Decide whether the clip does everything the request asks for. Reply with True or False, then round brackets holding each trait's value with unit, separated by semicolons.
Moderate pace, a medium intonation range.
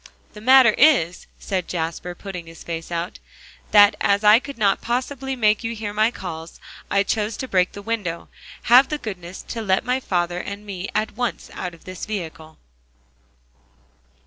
True (170 wpm; 4.4 semitones)